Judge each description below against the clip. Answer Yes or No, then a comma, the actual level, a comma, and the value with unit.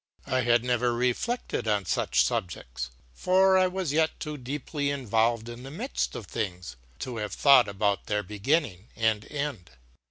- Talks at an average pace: Yes, average, 160 wpm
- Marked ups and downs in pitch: Yes, wide, 5.8 semitones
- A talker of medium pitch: No, low, 120 Hz